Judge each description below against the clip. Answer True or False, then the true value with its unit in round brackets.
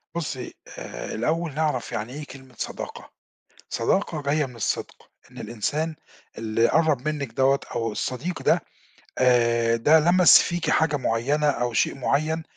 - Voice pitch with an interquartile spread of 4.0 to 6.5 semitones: True (4.8 semitones)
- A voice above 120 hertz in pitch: True (140 Hz)